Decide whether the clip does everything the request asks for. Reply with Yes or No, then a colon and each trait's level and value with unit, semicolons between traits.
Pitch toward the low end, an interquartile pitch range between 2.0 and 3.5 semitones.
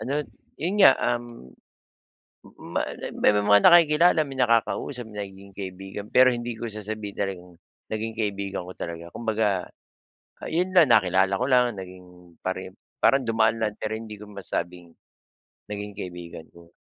No: low, 105 Hz; average, 4.1 semitones